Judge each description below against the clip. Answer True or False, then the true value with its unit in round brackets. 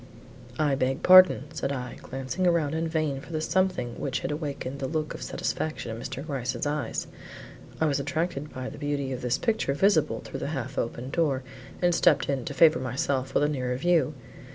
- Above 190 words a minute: True (200 wpm)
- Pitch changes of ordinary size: True (3.3 semitones)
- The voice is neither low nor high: True (145 Hz)